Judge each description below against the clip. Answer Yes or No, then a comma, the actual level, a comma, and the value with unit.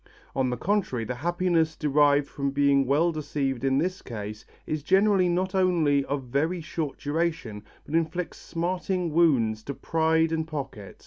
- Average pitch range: Yes, average, 4.0 semitones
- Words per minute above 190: No, average, 155 wpm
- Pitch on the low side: No, medium, 155 Hz